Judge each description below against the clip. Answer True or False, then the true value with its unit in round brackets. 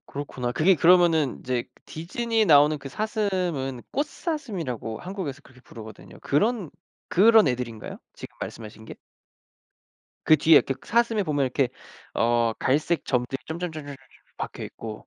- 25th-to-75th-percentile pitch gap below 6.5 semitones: False (7.0 semitones)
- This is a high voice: False (150 Hz)